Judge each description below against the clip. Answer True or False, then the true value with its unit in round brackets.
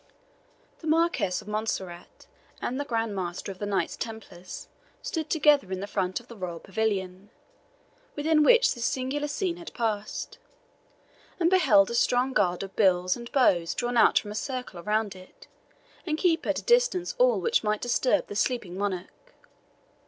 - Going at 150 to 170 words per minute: True (165 wpm)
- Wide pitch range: True (7.4 semitones)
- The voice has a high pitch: True (225 Hz)